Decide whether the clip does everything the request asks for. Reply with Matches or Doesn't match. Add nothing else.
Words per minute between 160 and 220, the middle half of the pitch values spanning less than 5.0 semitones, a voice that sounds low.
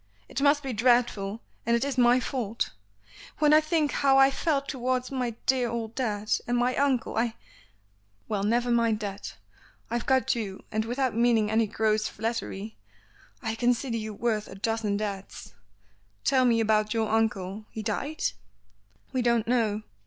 Doesn't match